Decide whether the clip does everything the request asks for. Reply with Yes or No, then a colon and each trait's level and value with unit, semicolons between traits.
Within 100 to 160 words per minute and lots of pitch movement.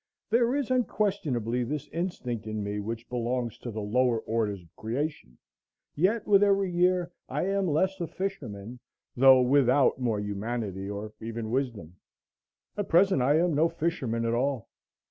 Yes: average, 155 wpm; wide, 7.7 semitones